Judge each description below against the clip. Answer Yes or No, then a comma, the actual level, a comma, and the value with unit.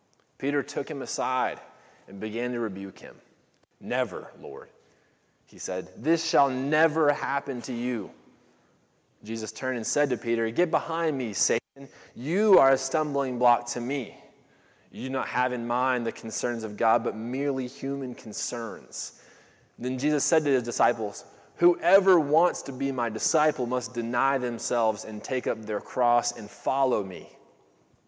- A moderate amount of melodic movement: Yes, average, 3.0 semitones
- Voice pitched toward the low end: Yes, low, 125 Hz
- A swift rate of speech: No, average, 155 wpm